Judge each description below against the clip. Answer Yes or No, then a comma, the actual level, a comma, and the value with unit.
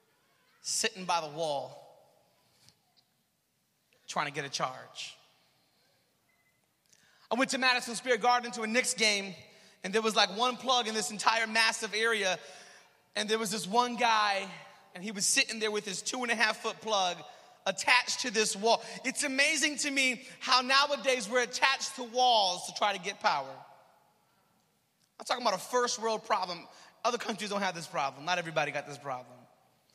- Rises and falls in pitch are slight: No, average, 4.2 semitones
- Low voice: No, high, 220 Hz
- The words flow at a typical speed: Yes, average, 170 wpm